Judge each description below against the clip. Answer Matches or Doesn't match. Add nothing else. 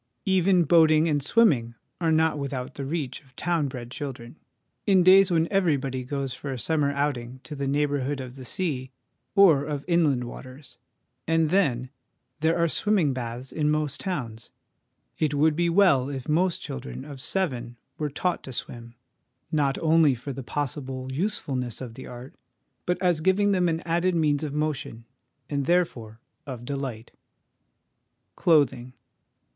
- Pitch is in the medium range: Matches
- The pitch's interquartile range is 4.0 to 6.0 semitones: Matches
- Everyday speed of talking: Matches